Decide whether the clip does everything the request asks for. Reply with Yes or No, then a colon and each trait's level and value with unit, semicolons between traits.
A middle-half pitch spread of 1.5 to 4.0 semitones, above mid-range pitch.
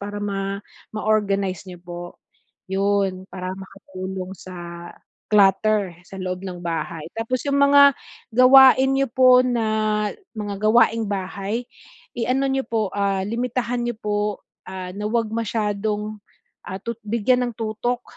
Yes: average, 3.3 semitones; high, 210 Hz